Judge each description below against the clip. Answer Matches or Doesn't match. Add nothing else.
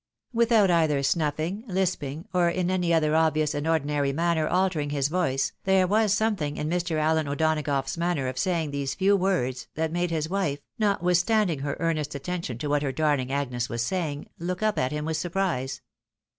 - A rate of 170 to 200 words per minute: Matches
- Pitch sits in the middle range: Matches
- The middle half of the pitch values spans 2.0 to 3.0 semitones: Doesn't match